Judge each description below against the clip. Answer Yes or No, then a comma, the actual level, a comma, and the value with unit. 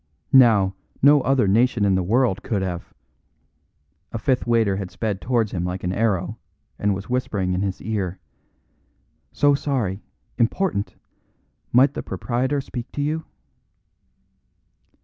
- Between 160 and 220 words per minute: No, average, 140 wpm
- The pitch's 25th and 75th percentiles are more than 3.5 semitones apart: Yes, average, 5.0 semitones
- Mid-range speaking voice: No, low, 110 Hz